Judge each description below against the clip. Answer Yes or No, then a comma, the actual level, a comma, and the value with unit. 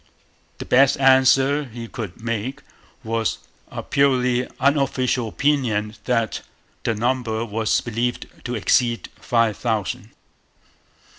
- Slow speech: Yes, slow, 105 wpm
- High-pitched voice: No, low, 120 Hz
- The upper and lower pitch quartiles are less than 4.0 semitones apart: Yes, average, 2.7 semitones